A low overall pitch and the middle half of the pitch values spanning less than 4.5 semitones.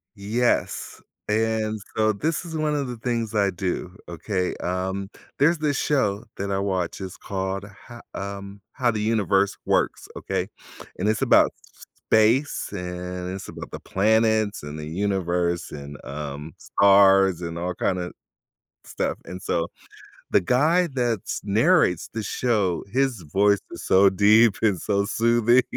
Yes: low, 100 Hz; average, 3.7 semitones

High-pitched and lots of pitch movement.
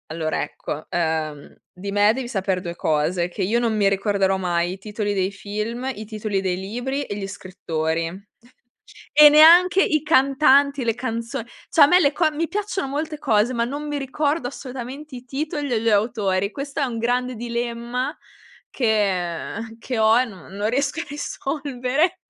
Yes: high, 235 Hz; wide, 6.0 semitones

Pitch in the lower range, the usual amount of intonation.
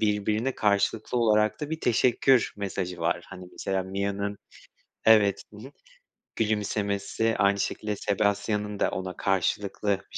No: low, 105 Hz; narrow, 1.7 semitones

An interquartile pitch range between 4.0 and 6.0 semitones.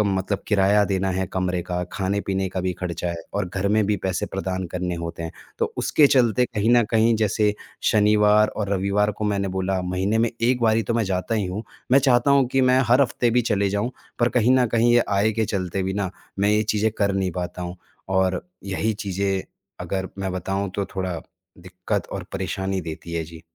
No: average, 2.9 semitones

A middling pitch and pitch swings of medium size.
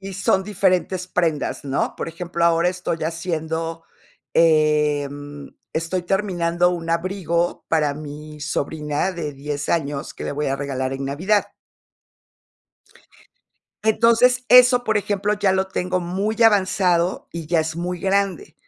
Yes: medium, 170 Hz; average, 3.9 semitones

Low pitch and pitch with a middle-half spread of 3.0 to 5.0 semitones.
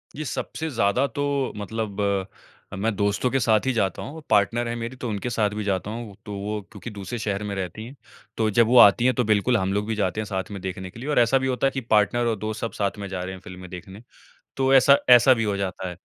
Yes: low, 110 Hz; average, 3.4 semitones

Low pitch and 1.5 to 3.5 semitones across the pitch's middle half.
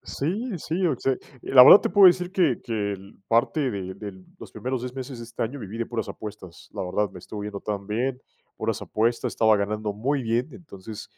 No: low, 115 Hz; average, 4.5 semitones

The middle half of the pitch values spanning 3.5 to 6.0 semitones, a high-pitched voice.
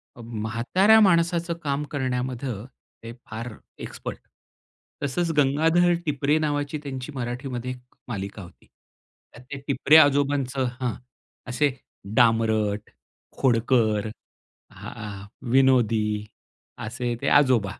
No: average, 4.1 semitones; low, 130 Hz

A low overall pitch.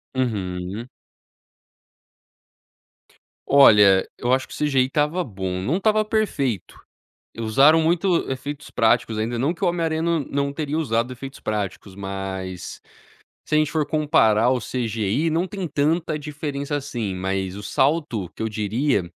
Yes: low, 130 Hz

